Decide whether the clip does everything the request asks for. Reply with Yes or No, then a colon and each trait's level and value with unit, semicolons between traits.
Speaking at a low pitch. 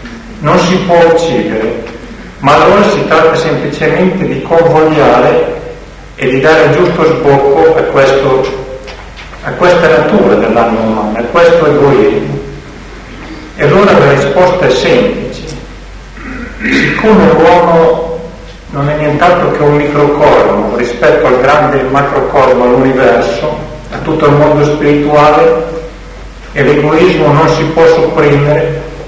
No: medium, 150 Hz